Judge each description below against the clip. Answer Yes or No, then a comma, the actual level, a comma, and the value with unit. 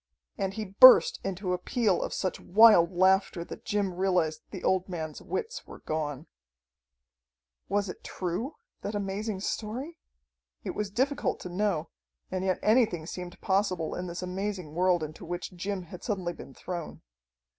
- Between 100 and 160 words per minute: Yes, average, 155 wpm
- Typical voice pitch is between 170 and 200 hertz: Yes, high, 190 Hz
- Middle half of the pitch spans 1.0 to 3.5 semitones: Yes, average, 2.9 semitones